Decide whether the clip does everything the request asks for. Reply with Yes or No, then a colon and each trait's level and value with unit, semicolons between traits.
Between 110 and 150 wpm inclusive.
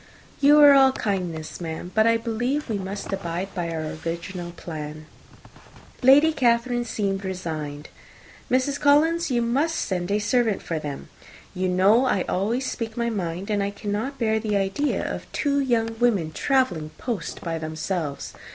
No: average, 160 wpm